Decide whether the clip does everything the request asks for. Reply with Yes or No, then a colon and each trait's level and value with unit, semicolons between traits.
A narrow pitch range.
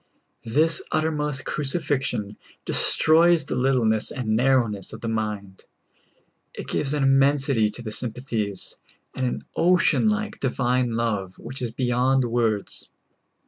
No: average, 4.2 semitones